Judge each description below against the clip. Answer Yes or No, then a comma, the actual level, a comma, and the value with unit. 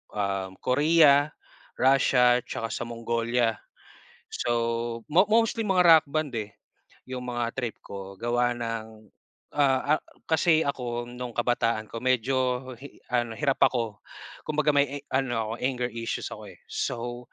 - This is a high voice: No, low, 120 Hz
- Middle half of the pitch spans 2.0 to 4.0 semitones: Yes, average, 3.3 semitones